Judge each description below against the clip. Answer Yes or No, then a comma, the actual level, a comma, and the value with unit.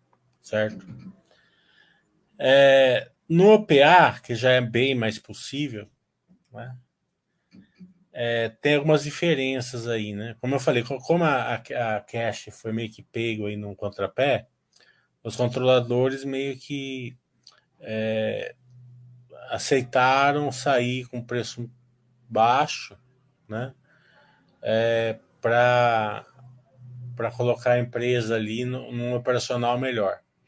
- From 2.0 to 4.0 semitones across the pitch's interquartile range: Yes, narrow, 2.6 semitones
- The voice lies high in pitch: No, low, 125 Hz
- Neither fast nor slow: No, slow, 105 wpm